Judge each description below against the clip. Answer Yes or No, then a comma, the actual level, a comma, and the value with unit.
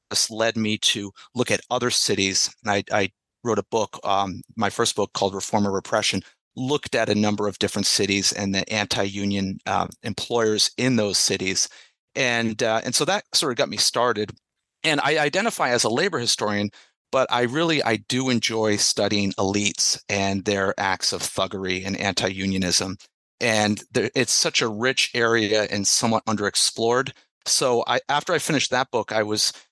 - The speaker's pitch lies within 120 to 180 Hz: No, low, 105 Hz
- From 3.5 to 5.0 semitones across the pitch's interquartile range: No, average, 2.7 semitones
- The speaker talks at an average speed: Yes, average, 180 wpm